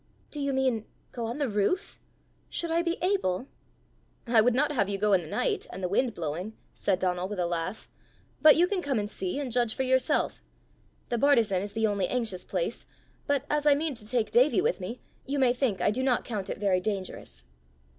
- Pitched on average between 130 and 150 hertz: No, high, 230 Hz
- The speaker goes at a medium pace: No, fast, 215 wpm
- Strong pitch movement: Yes, wide, 5.9 semitones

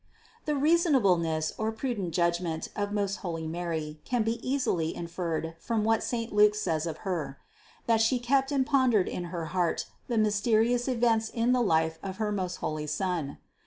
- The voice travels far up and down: Yes, wide, 5.8 semitones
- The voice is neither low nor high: No, high, 205 Hz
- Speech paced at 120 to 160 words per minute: No, average, 170 wpm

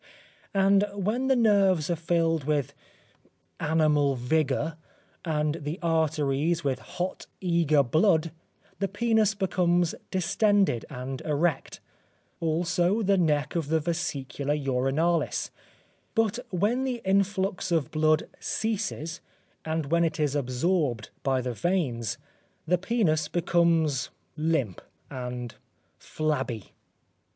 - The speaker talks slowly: Yes, slow, 110 wpm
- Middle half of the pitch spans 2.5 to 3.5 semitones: No, average, 4.4 semitones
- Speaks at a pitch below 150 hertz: No, medium, 160 Hz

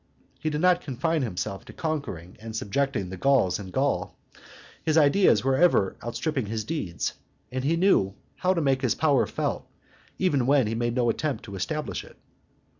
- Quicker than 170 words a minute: Yes, average, 185 wpm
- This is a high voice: No, low, 130 Hz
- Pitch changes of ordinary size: No, wide, 6.4 semitones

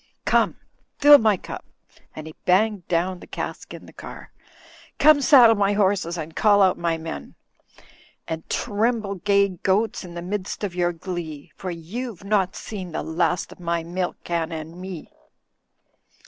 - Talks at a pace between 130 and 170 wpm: Yes, average, 165 wpm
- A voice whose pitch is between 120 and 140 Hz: No, medium, 185 Hz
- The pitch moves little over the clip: No, average, 3.4 semitones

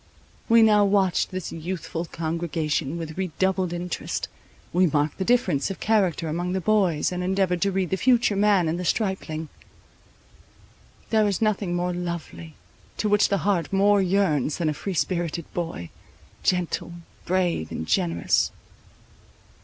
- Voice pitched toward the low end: No, medium, 180 Hz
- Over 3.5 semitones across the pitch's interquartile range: No, average, 3.1 semitones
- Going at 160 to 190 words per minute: No, average, 145 wpm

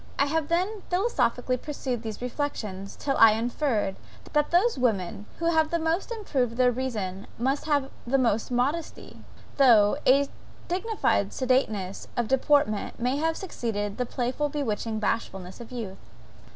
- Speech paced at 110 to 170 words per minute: Yes, average, 140 wpm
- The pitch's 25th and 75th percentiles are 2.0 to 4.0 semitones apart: No, average, 5.2 semitones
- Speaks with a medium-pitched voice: No, very high, 255 Hz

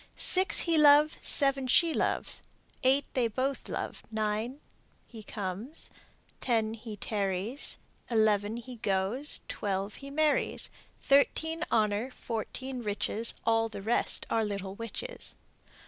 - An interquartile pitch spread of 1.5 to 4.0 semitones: No, average, 4.6 semitones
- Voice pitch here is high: Yes, high, 230 Hz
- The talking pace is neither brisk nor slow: No, slow, 120 wpm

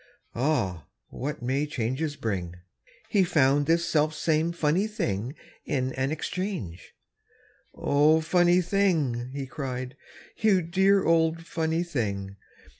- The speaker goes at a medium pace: No, slow, 115 wpm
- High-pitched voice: No, medium, 150 Hz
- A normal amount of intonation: Yes, average, 4.9 semitones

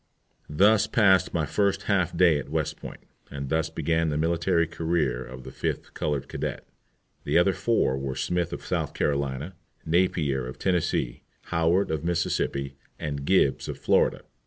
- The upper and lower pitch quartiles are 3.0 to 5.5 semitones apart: Yes, average, 4.1 semitones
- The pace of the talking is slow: No, average, 160 wpm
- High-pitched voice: No, very low, 80 Hz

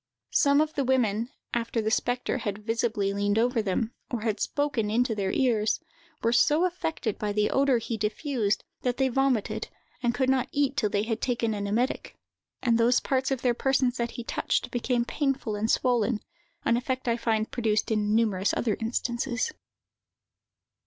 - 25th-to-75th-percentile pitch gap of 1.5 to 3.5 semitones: Yes, average, 3.1 semitones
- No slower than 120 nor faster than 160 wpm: No, average, 175 wpm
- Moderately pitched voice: No, high, 235 Hz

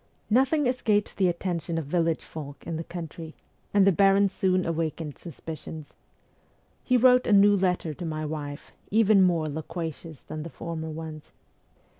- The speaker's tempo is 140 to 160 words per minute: Yes, average, 155 wpm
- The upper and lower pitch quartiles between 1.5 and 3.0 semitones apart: No, average, 3.8 semitones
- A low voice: No, medium, 170 Hz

